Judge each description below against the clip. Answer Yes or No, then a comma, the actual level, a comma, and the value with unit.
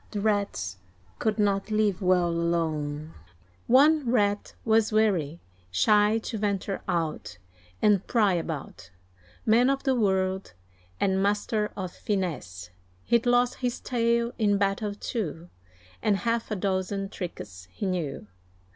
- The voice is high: Yes, high, 200 Hz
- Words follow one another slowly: Yes, slow, 130 wpm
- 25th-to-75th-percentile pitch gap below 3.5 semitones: No, average, 4.0 semitones